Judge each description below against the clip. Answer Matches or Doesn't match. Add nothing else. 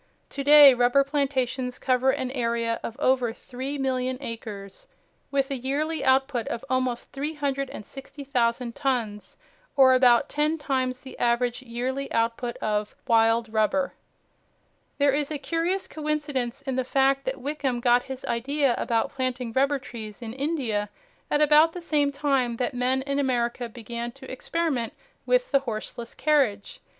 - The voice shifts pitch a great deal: Doesn't match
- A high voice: Matches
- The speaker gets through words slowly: Doesn't match